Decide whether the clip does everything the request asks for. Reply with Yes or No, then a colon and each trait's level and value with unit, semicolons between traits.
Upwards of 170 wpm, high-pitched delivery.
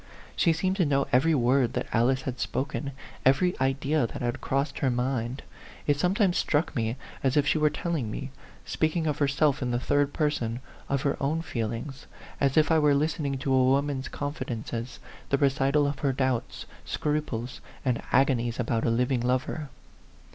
No: average, 180 wpm; low, 135 Hz